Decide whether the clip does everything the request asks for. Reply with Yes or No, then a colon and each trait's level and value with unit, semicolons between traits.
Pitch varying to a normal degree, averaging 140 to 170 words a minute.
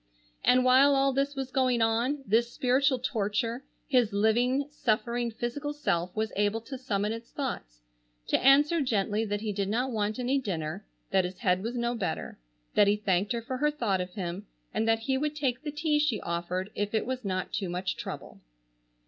No: average, 4.4 semitones; average, 195 wpm